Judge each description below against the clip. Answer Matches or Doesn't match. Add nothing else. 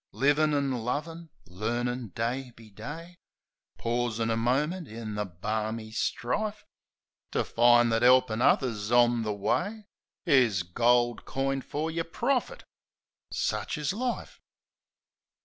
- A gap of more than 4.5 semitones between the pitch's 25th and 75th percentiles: Matches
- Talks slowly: Matches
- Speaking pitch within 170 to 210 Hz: Doesn't match